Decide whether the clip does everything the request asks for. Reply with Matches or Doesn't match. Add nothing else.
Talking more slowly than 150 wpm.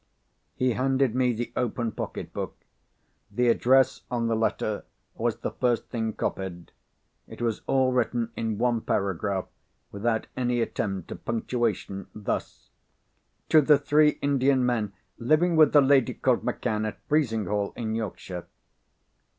Matches